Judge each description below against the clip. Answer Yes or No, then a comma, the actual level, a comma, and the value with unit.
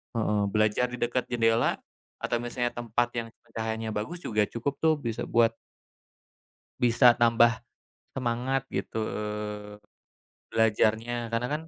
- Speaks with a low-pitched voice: Yes, low, 115 Hz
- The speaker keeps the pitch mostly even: Yes, narrow, 1.4 semitones